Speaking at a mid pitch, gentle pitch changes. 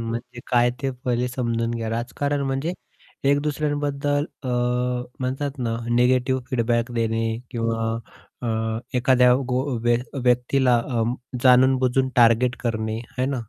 No: low, 125 Hz; narrow, 2.2 semitones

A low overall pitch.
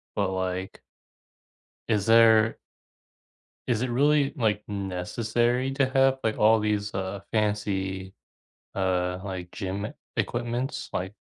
Yes: low, 105 Hz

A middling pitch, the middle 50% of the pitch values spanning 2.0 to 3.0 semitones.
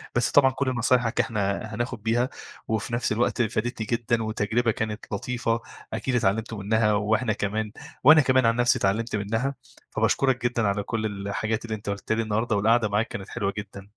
No: low, 110 Hz; narrow, 2.4 semitones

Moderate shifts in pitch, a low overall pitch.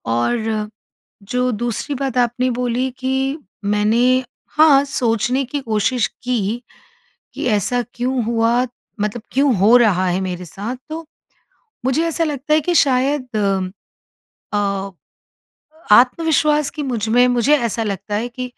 No: average, 3.5 semitones; high, 245 Hz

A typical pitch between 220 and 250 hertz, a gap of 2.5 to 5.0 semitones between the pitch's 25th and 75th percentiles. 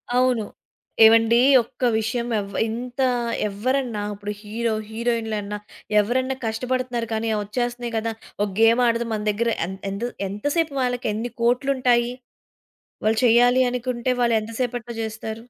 No: high, 235 Hz; narrow, 2.0 semitones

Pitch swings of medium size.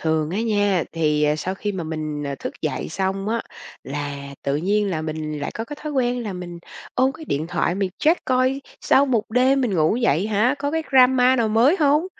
No: wide, 8.2 semitones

